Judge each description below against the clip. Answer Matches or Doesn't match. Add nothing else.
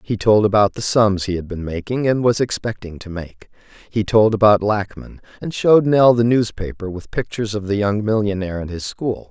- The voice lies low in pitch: Matches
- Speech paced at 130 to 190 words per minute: Doesn't match